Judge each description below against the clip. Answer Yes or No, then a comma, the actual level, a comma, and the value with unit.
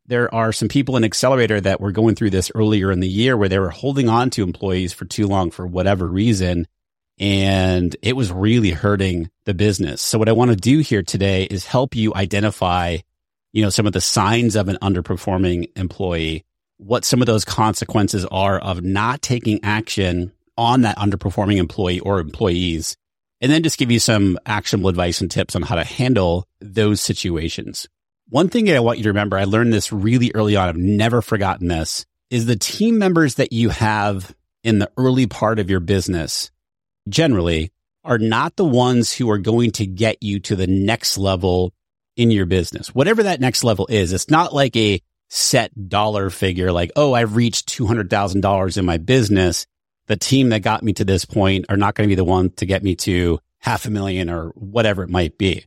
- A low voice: Yes, low, 100 Hz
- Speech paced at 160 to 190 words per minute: No, average, 200 wpm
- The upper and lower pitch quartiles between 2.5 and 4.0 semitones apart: Yes, average, 3.7 semitones